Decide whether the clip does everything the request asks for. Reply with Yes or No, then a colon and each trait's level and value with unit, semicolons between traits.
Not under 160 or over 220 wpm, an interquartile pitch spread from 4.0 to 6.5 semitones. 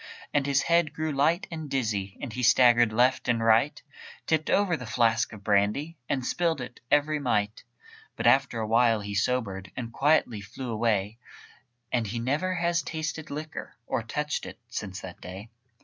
Yes: average, 170 wpm; average, 5.3 semitones